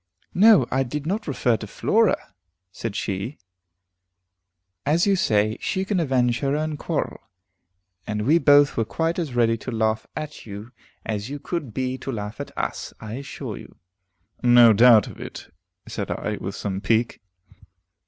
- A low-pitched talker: Yes, low, 125 Hz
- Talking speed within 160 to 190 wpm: Yes, average, 165 wpm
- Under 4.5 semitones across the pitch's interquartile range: No, wide, 5.4 semitones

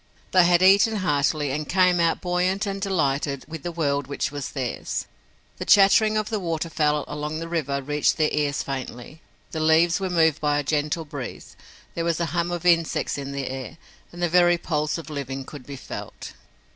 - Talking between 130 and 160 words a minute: No, average, 195 wpm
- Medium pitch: Yes, medium, 160 Hz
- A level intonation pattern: No, average, 3.4 semitones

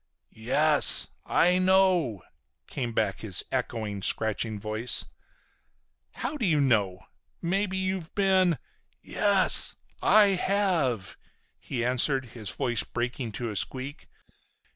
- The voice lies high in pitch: No, low, 130 Hz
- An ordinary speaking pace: No, slow, 110 wpm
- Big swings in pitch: Yes, wide, 8.8 semitones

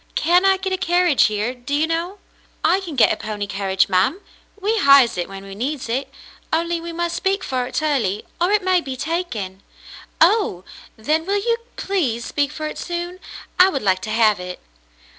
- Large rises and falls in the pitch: Yes, wide, 8.5 semitones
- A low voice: No, very high, 300 Hz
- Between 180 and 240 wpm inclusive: Yes, average, 200 wpm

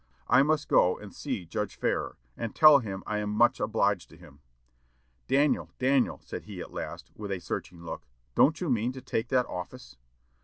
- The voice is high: No, low, 110 Hz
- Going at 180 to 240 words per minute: Yes, average, 190 wpm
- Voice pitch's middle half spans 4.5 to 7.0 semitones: Yes, wide, 5.4 semitones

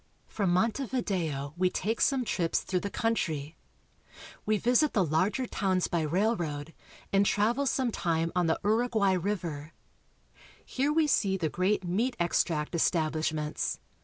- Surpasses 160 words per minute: No, slow, 135 wpm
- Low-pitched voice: No, medium, 185 Hz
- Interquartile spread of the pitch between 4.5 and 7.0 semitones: Yes, wide, 5.6 semitones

